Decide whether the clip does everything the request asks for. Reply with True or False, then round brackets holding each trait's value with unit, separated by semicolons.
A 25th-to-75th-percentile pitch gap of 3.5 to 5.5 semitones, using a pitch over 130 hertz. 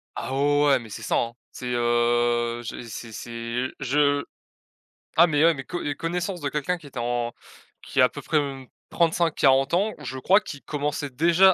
True (4.9 semitones; 140 Hz)